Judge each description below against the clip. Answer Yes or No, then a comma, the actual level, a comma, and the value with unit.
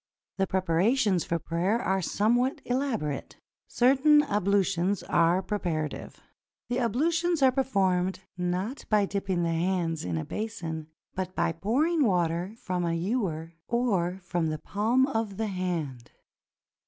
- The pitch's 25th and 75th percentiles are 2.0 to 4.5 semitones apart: No, wide, 5.5 semitones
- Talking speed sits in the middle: No, slow, 130 wpm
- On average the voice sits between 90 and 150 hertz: No, high, 190 Hz